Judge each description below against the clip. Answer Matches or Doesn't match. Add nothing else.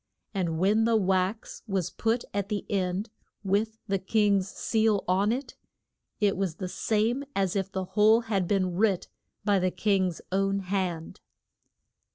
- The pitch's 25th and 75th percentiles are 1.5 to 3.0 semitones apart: Matches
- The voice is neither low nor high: Doesn't match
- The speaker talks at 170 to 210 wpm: Doesn't match